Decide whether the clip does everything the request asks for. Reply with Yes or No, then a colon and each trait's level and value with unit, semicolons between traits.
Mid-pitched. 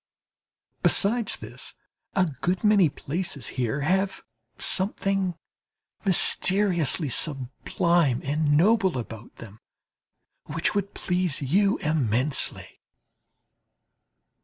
Yes: medium, 170 Hz